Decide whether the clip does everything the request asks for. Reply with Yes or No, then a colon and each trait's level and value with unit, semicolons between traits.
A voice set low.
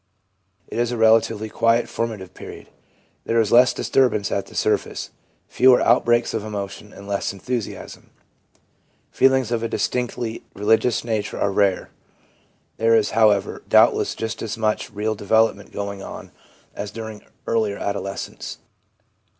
Yes: low, 110 Hz